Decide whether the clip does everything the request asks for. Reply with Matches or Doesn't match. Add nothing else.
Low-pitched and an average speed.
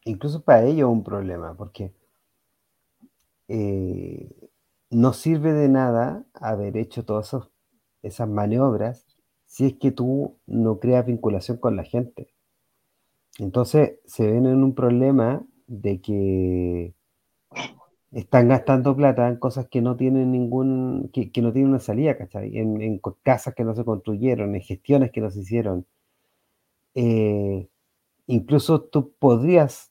Matches